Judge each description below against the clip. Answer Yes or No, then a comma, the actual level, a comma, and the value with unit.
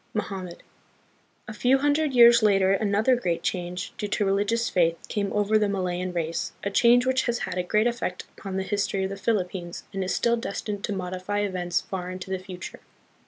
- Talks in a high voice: Yes, high, 200 Hz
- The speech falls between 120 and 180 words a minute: No, average, 195 wpm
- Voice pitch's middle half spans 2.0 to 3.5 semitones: Yes, average, 3.0 semitones